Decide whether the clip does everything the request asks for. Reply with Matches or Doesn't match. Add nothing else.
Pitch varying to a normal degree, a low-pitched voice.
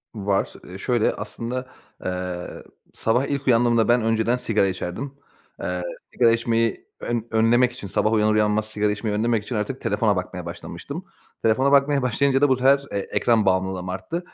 Matches